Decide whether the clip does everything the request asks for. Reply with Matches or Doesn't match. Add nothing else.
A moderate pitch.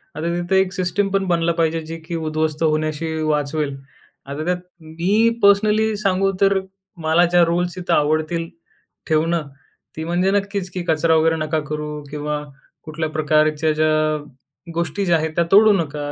Matches